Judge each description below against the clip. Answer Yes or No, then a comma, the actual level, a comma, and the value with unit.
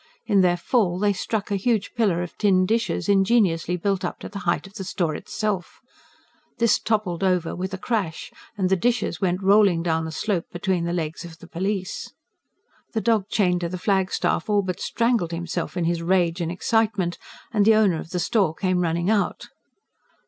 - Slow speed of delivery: No, average, 190 wpm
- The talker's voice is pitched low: No, medium, 185 Hz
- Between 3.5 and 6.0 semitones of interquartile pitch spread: No, average, 3.1 semitones